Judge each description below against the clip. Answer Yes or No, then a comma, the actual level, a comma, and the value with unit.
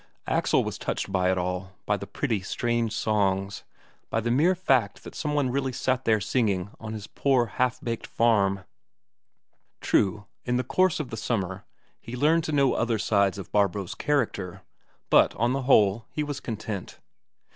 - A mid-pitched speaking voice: No, low, 115 Hz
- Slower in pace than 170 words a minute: No, average, 175 wpm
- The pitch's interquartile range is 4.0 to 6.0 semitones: Yes, average, 4.7 semitones